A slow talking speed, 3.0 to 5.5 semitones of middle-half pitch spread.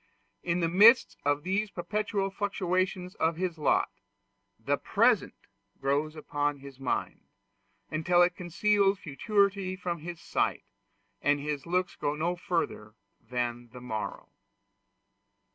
Yes: slow, 125 wpm; average, 4.8 semitones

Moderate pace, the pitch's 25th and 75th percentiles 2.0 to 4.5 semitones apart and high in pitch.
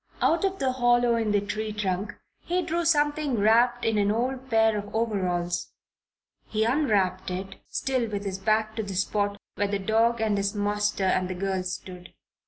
Yes: average, 185 wpm; average, 3.5 semitones; high, 215 Hz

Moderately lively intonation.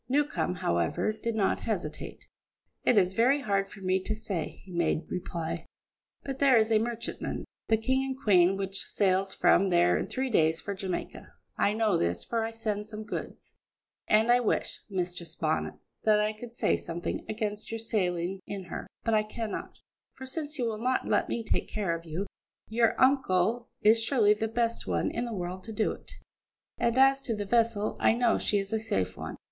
Yes: average, 3.7 semitones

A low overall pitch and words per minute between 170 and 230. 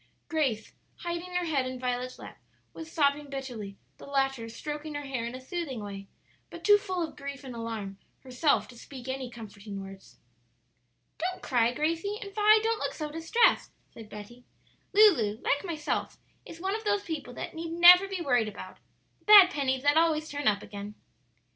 No: very high, 280 Hz; average, 180 wpm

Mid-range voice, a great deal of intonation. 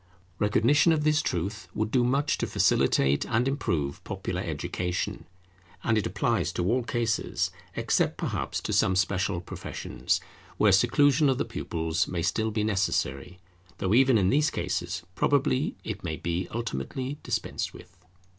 No: low, 105 Hz; wide, 6.3 semitones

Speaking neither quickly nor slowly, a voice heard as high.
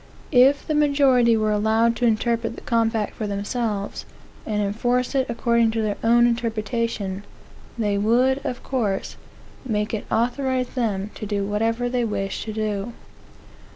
Yes: average, 150 wpm; high, 230 Hz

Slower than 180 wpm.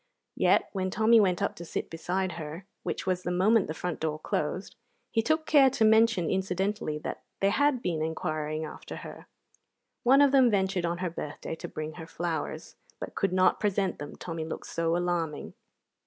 No: average, 185 wpm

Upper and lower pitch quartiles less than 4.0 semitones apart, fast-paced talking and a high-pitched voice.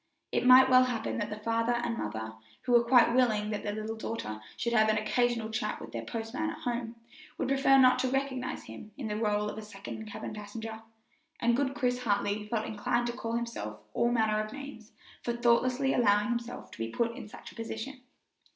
Yes: narrow, 2.6 semitones; fast, 210 wpm; high, 230 Hz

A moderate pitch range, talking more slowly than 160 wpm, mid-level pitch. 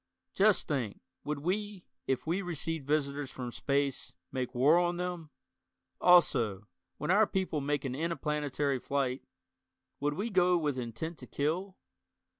Yes: average, 4.4 semitones; average, 140 wpm; medium, 150 Hz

